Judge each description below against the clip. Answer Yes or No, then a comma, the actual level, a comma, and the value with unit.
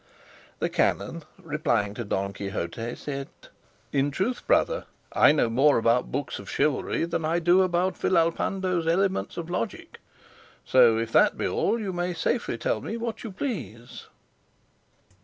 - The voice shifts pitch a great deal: Yes, wide, 7.8 semitones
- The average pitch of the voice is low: No, medium, 160 Hz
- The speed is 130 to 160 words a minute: Yes, average, 150 wpm